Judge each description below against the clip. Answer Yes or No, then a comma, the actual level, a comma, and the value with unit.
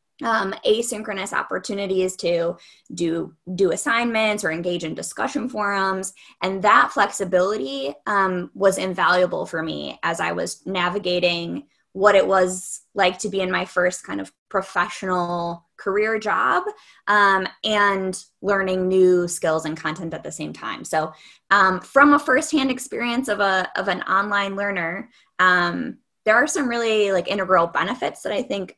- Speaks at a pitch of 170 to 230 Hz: Yes, high, 190 Hz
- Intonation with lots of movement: No, average, 2.9 semitones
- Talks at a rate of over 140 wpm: Yes, average, 150 wpm